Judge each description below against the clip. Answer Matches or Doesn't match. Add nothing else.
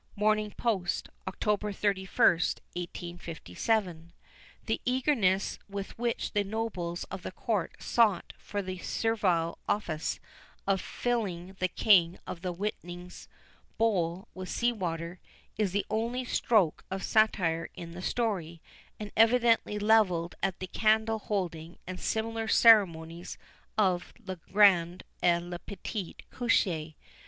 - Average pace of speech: Doesn't match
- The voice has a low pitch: Doesn't match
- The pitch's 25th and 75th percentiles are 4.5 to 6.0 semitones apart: Doesn't match